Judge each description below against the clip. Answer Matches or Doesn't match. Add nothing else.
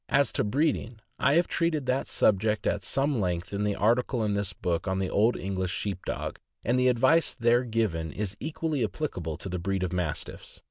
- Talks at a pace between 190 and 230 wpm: Matches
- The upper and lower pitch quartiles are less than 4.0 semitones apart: Doesn't match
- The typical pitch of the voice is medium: Doesn't match